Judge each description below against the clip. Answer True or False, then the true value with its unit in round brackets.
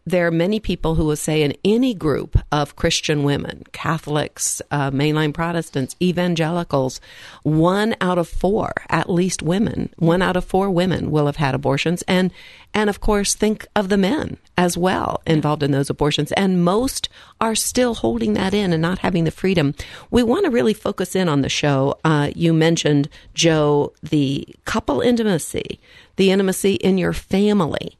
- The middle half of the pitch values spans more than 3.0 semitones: True (4.2 semitones)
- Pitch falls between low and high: True (170 Hz)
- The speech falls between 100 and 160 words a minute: False (175 wpm)